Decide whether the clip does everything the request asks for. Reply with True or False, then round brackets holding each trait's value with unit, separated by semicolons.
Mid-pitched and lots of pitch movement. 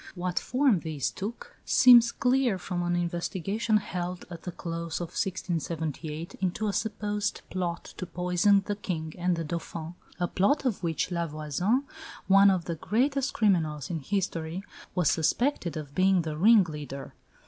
False (180 Hz; 3.8 semitones)